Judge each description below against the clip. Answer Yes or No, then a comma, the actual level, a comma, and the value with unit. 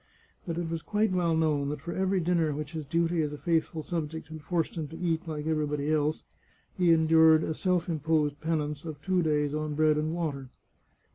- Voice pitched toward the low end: No, medium, 160 Hz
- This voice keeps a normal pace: No, fast, 210 wpm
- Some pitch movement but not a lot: No, narrow, 1.9 semitones